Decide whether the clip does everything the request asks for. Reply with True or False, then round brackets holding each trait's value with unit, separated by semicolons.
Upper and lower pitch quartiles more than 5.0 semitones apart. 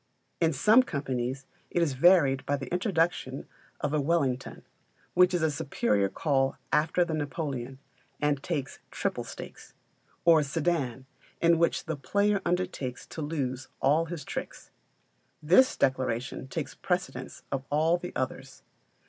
False (4.2 semitones)